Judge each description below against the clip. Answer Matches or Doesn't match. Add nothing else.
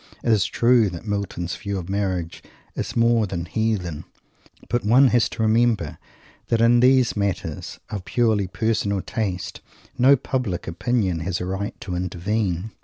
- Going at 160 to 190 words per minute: Doesn't match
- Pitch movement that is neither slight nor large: Matches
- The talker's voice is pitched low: Matches